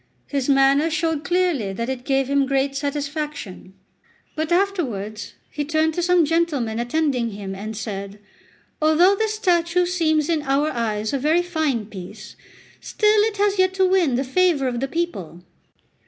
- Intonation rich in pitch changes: Yes, wide, 6.2 semitones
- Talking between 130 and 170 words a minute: Yes, average, 160 wpm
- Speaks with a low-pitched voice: No, very high, 290 Hz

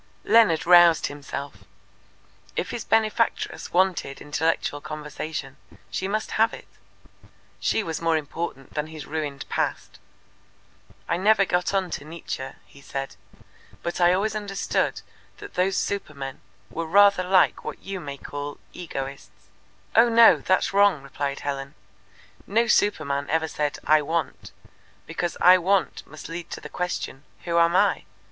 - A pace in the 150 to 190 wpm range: No, average, 140 wpm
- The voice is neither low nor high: Yes, medium, 165 Hz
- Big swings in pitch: No, average, 5.0 semitones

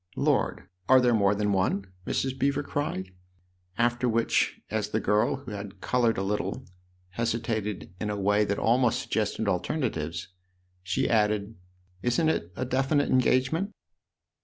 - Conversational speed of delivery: Yes, average, 160 wpm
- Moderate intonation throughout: Yes, average, 4.2 semitones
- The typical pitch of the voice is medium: No, low, 110 Hz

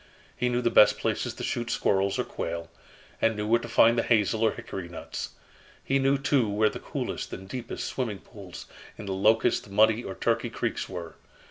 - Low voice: Yes, low, 110 Hz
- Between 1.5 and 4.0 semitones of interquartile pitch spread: Yes, average, 3.4 semitones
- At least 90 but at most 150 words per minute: No, average, 200 wpm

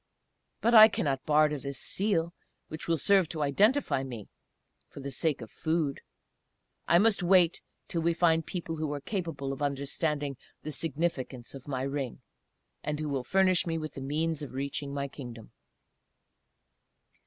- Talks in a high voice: No, medium, 150 Hz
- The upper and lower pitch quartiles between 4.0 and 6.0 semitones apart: No, average, 3.5 semitones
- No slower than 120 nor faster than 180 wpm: Yes, average, 160 wpm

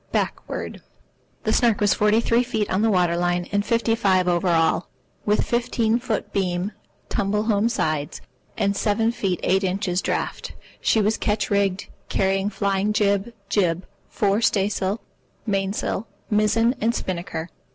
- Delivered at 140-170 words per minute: Yes, average, 150 wpm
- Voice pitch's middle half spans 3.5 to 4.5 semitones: No, narrow, 2.6 semitones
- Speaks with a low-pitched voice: No, high, 200 Hz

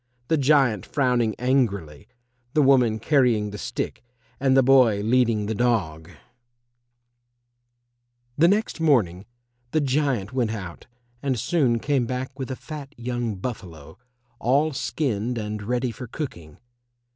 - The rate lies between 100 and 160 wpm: Yes, slow, 135 wpm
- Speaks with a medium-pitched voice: No, low, 125 Hz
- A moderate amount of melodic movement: Yes, average, 4.3 semitones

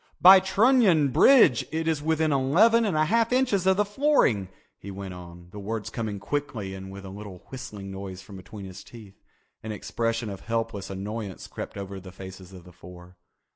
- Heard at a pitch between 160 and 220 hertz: No, low, 110 Hz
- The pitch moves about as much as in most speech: No, wide, 8.8 semitones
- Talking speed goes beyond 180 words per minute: Yes, average, 190 wpm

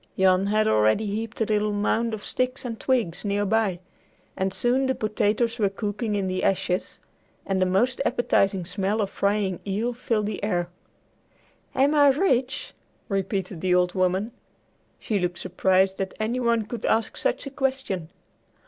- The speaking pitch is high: Yes, high, 210 Hz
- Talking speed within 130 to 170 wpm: Yes, average, 165 wpm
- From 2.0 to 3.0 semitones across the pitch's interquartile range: No, average, 3.7 semitones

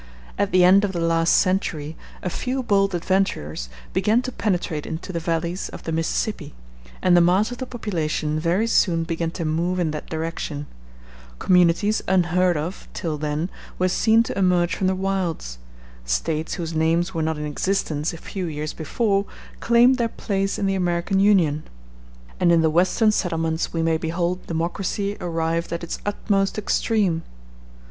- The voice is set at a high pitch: No, medium, 175 Hz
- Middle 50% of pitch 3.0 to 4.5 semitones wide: Yes, average, 3.3 semitones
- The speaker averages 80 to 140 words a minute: No, average, 170 wpm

